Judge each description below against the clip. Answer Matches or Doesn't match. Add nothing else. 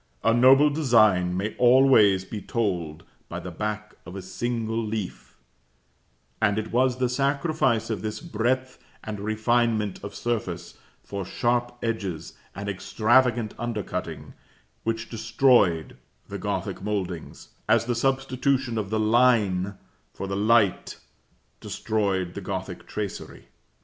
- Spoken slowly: Matches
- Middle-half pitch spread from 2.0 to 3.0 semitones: Doesn't match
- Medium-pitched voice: Doesn't match